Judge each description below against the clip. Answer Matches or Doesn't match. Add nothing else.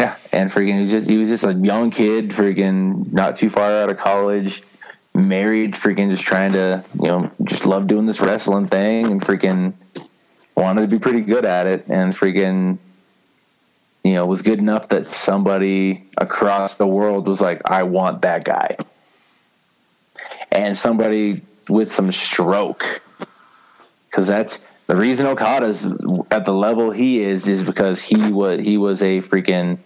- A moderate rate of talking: Matches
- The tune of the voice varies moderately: Doesn't match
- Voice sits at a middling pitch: Doesn't match